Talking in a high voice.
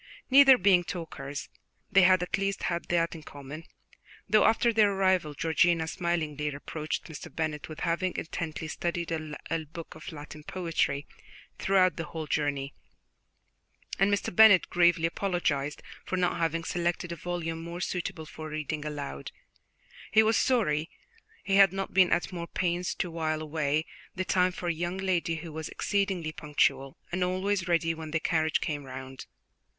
No: medium, 170 Hz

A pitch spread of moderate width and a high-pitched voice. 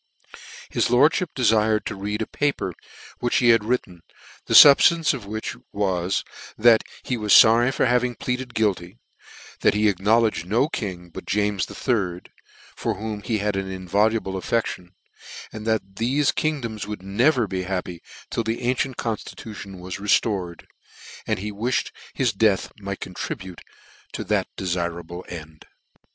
No: average, 3.8 semitones; low, 105 Hz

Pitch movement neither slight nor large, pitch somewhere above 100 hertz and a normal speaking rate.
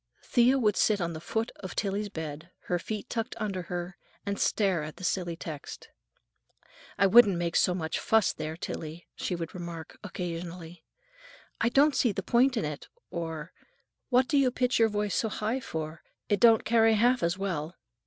Yes: average, 4.9 semitones; high, 190 Hz; average, 185 wpm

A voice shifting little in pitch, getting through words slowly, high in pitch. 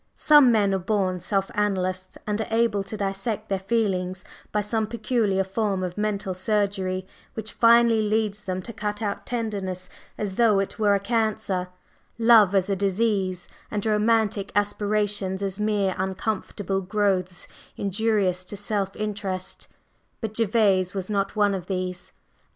No: narrow, 2.2 semitones; average, 150 wpm; high, 205 Hz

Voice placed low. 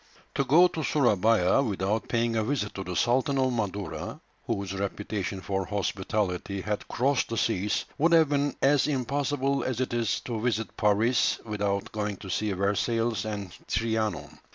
Yes: low, 110 Hz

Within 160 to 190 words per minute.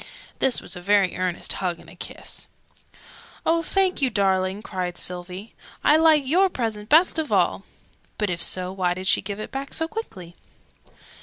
Yes: average, 175 wpm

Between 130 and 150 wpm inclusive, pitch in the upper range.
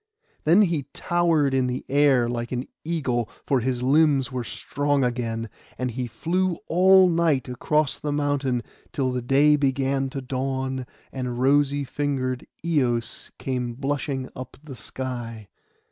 No: average, 145 wpm; low, 135 Hz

